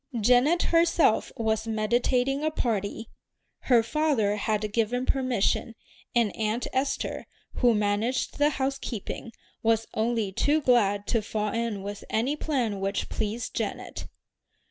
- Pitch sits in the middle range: No, high, 230 Hz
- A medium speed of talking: No, slow, 125 wpm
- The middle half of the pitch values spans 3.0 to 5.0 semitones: Yes, average, 3.4 semitones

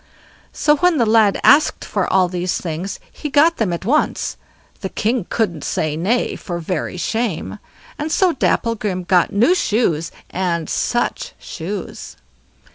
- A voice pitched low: No, high, 205 Hz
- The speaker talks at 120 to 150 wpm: Yes, average, 140 wpm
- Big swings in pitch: Yes, wide, 5.7 semitones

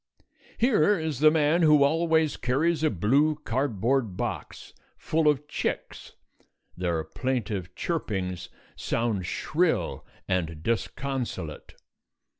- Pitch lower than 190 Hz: Yes, low, 135 Hz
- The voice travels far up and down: Yes, wide, 7.7 semitones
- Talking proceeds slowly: Yes, slow, 100 wpm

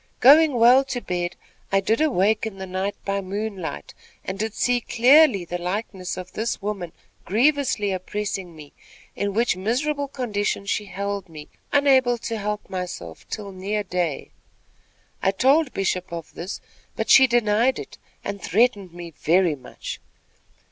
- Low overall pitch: No, high, 200 Hz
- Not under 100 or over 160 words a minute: Yes, average, 150 wpm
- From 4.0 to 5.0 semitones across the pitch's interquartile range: Yes, average, 4.6 semitones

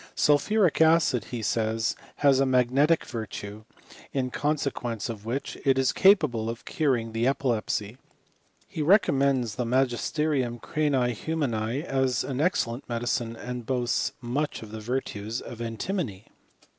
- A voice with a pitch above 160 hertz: No, low, 125 Hz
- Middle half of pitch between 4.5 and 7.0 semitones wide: No, average, 3.8 semitones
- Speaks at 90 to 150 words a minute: Yes, average, 140 wpm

